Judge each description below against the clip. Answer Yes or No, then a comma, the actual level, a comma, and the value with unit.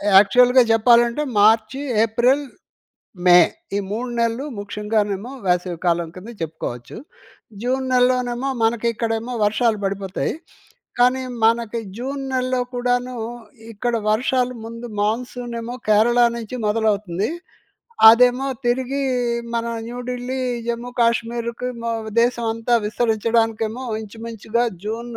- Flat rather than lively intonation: Yes, narrow, 2.3 semitones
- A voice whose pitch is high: Yes, high, 235 Hz